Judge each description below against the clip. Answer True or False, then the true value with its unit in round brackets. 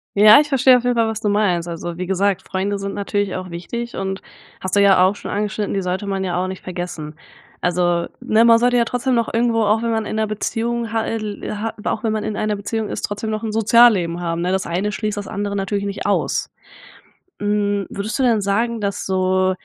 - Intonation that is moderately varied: True (3.0 semitones)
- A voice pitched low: False (205 Hz)